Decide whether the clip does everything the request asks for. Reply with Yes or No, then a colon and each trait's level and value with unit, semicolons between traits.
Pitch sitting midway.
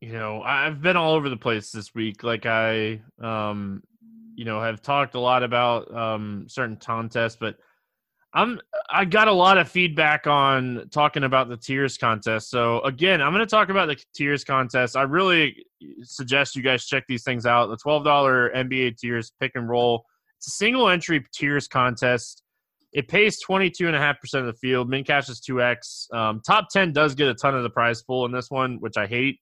No: low, 130 Hz